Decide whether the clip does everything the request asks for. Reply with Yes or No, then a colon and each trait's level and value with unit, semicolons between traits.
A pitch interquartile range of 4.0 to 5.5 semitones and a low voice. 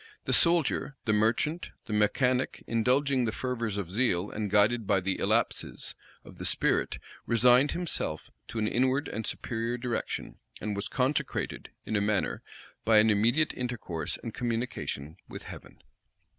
No: average, 3.4 semitones; low, 115 Hz